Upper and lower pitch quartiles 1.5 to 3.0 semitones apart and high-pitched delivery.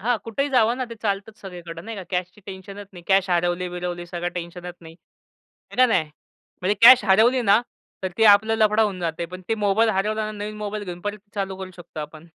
No: average, 3.4 semitones; high, 195 Hz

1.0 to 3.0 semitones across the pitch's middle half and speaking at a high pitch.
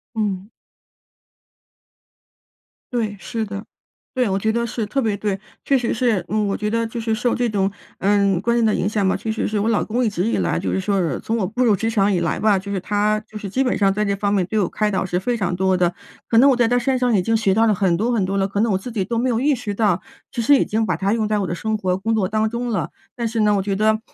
Yes: average, 2.7 semitones; high, 215 Hz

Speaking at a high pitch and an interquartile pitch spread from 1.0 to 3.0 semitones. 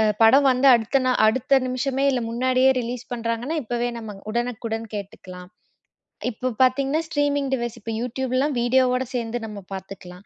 Yes: high, 245 Hz; average, 2.7 semitones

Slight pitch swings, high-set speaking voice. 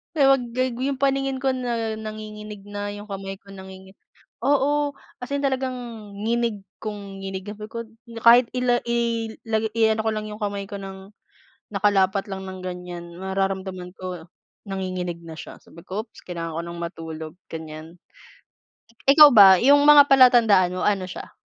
No: average, 4.0 semitones; high, 205 Hz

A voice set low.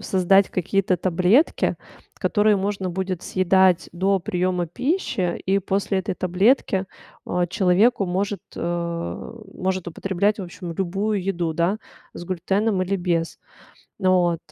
No: medium, 185 Hz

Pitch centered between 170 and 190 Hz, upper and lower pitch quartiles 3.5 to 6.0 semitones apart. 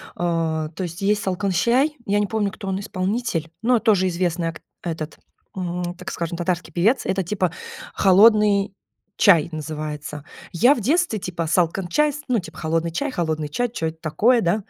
Yes: medium, 185 Hz; average, 4.2 semitones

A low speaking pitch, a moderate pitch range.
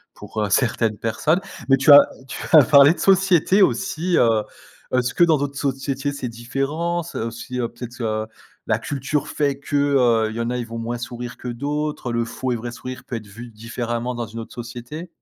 Yes: low, 125 Hz; average, 3.6 semitones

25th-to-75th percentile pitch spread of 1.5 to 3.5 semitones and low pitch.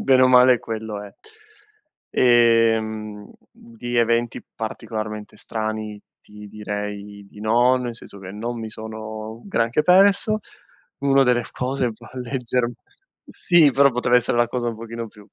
Yes: narrow, 2.5 semitones; low, 115 Hz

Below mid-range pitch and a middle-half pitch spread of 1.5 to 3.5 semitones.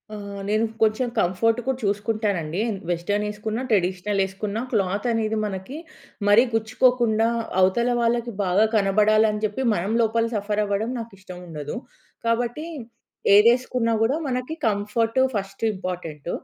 No: high, 210 Hz; average, 2.7 semitones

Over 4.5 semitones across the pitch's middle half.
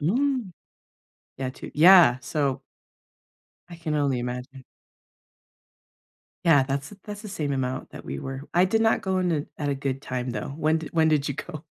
Yes: average, 5.0 semitones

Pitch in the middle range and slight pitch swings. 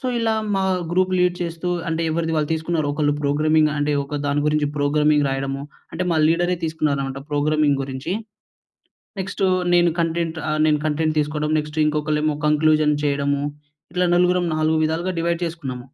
Yes: medium, 155 Hz; narrow, 2.2 semitones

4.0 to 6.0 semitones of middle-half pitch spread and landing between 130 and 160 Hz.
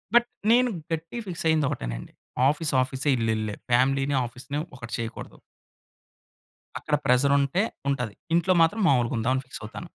Yes: average, 5.0 semitones; low, 135 Hz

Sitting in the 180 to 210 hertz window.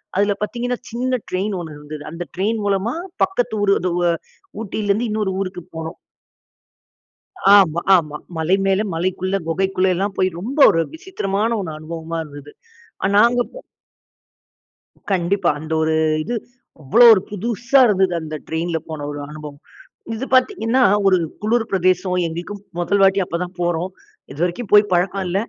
Yes: high, 190 Hz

